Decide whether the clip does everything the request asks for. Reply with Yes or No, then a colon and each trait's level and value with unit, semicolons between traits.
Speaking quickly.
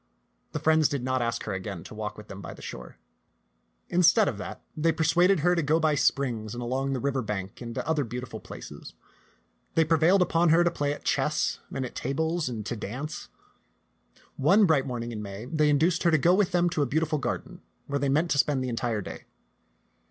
Yes: fast, 215 wpm